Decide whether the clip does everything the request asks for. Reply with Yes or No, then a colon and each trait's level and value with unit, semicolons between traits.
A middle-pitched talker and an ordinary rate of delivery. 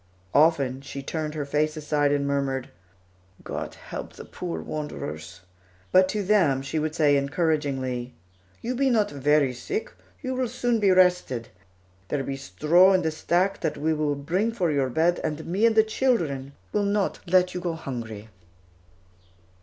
Yes: medium, 155 Hz; average, 165 wpm